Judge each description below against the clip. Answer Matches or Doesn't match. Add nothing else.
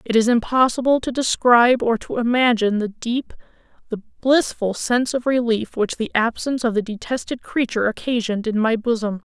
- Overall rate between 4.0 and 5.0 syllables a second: Doesn't match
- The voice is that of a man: Doesn't match